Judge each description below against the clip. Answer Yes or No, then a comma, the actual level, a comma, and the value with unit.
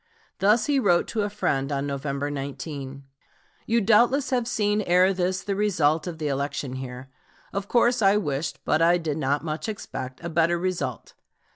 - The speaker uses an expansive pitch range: Yes, wide, 6.6 semitones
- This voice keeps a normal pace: Yes, average, 175 wpm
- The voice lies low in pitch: No, medium, 170 Hz